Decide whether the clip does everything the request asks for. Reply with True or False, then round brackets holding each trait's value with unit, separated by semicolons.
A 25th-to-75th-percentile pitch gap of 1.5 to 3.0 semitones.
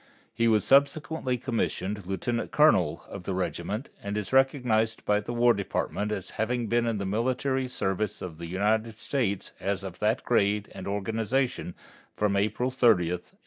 False (3.7 semitones)